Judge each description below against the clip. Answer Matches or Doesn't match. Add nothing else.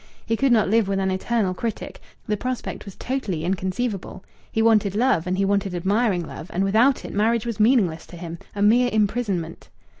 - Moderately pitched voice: Doesn't match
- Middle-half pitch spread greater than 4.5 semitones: Doesn't match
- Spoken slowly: Doesn't match